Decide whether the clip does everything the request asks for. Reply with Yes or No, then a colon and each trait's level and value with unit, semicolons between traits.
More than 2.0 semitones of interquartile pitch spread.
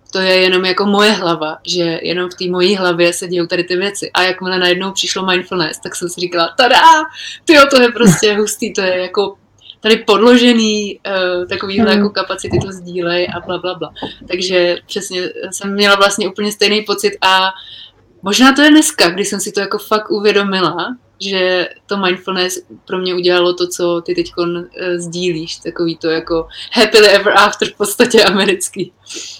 Yes: narrow, 2.5 semitones